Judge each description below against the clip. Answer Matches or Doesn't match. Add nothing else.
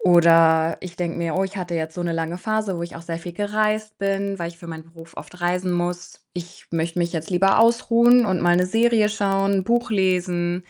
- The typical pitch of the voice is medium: Matches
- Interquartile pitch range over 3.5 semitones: Doesn't match